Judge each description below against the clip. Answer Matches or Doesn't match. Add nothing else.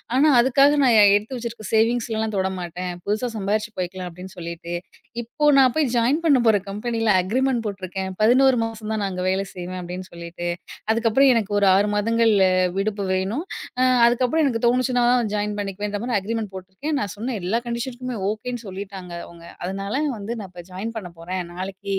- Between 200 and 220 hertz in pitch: Matches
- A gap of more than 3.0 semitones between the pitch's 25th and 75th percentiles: Matches